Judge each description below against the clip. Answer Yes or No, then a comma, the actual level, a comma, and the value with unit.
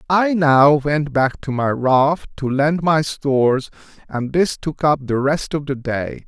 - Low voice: No, medium, 145 Hz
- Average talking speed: Yes, average, 190 wpm